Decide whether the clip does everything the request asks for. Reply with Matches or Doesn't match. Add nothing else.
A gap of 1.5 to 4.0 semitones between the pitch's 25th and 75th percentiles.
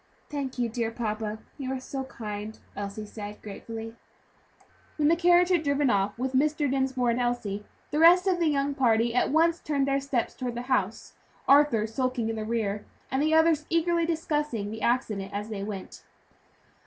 Doesn't match